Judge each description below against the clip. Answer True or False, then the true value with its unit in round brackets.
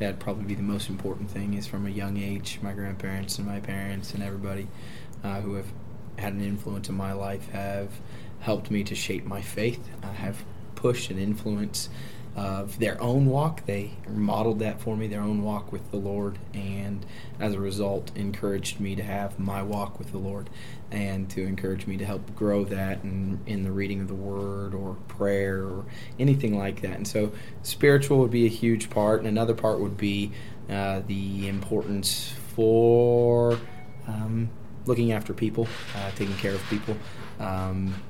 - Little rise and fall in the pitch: True (2.0 semitones)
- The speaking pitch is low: True (100 Hz)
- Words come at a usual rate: True (185 wpm)